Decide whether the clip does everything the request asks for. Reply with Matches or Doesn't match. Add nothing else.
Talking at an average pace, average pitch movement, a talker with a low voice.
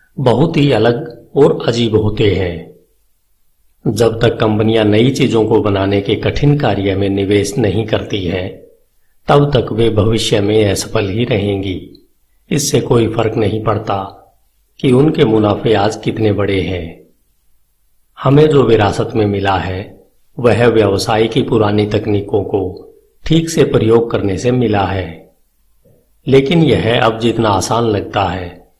Matches